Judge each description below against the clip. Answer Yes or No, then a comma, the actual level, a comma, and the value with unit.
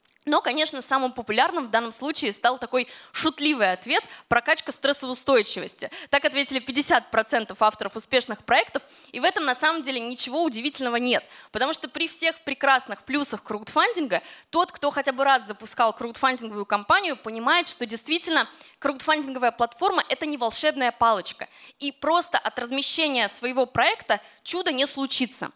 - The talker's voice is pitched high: Yes, very high, 265 Hz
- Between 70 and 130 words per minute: No, average, 145 wpm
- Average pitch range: Yes, average, 4.5 semitones